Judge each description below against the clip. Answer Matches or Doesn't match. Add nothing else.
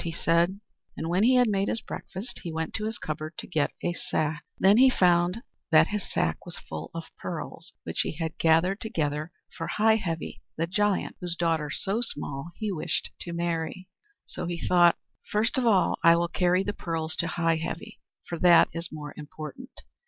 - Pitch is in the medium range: Matches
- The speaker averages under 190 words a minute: Doesn't match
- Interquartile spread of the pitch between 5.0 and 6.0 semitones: Doesn't match